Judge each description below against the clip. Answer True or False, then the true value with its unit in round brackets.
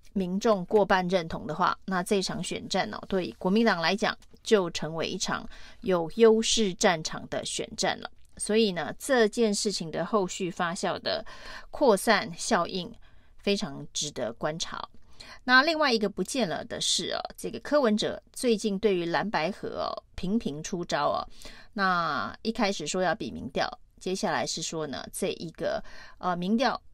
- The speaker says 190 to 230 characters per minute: False (240 characters per minute)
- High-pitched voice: True (205 Hz)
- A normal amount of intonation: True (3.4 semitones)